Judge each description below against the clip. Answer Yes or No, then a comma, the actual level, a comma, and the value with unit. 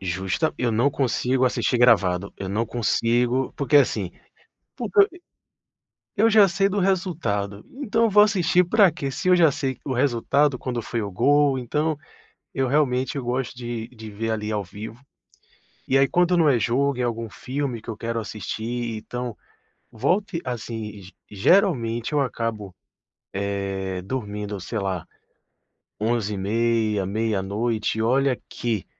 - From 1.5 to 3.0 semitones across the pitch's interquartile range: No, average, 4.7 semitones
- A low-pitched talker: Yes, low, 120 Hz